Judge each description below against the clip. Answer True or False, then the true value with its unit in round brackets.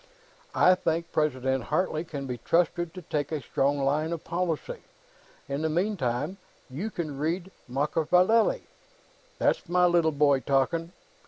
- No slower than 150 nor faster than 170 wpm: False (140 wpm)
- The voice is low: False (160 Hz)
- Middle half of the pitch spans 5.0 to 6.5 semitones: False (3.9 semitones)